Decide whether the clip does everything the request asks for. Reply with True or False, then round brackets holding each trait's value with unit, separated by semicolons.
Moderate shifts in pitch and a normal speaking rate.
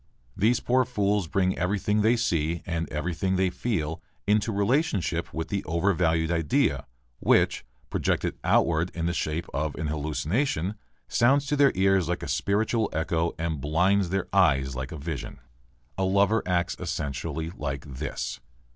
True (4.2 semitones; 150 wpm)